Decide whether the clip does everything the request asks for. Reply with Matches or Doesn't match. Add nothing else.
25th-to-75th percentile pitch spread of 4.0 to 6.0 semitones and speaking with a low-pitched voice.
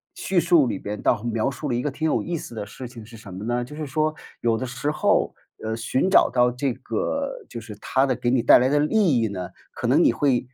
Matches